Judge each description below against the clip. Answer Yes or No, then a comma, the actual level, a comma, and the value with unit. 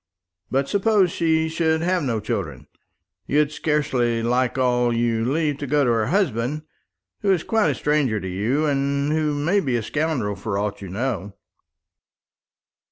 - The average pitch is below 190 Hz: Yes, medium, 140 Hz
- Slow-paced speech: No, average, 165 wpm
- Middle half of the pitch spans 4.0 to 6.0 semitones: Yes, average, 5.2 semitones